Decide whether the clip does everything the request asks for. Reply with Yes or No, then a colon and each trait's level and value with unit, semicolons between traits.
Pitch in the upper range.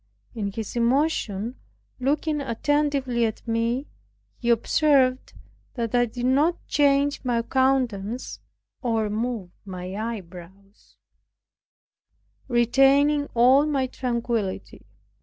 Yes: high, 245 Hz